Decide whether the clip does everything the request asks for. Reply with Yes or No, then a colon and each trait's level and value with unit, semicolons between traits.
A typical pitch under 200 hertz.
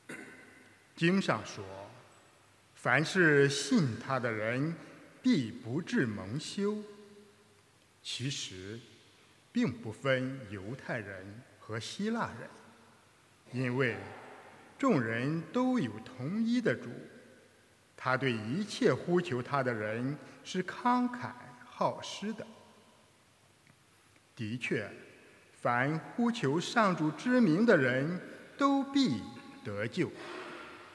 Yes: low, 135 Hz